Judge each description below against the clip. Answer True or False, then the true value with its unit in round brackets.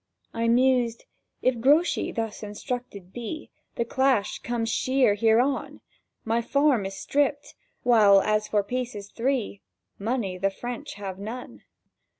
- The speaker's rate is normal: False (130 wpm)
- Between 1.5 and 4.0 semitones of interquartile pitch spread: True (3.6 semitones)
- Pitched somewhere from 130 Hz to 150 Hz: False (230 Hz)